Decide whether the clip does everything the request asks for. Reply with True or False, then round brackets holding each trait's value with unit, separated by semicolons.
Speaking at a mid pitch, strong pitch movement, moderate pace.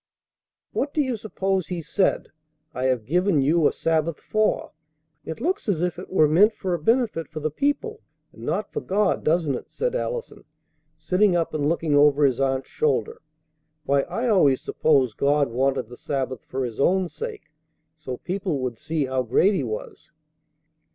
True (165 Hz; 6.9 semitones; 180 wpm)